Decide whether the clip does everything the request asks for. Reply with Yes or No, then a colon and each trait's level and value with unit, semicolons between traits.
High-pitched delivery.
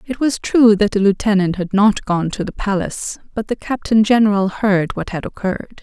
Yes: high, 205 Hz